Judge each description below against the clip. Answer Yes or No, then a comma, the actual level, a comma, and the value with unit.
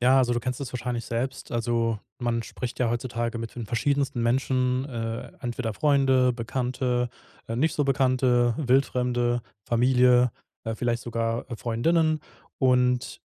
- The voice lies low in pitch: Yes, low, 125 Hz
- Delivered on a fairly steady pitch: Yes, narrow, 1.7 semitones